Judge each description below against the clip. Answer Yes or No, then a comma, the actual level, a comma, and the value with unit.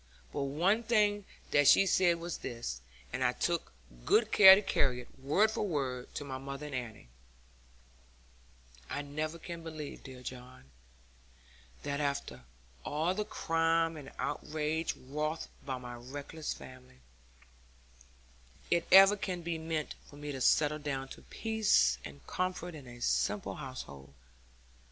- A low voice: No, medium, 150 Hz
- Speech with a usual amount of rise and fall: Yes, average, 4.8 semitones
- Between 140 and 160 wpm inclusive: Yes, average, 145 wpm